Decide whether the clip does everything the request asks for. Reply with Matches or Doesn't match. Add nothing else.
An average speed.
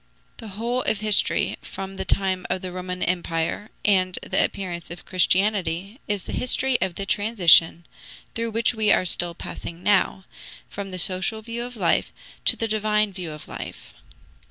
Matches